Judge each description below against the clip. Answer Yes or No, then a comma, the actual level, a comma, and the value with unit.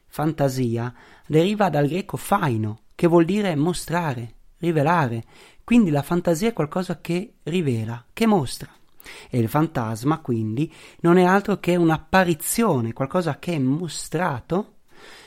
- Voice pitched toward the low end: No, medium, 165 Hz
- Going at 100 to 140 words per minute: Yes, average, 125 wpm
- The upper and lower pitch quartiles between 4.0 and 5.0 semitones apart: No, wide, 5.4 semitones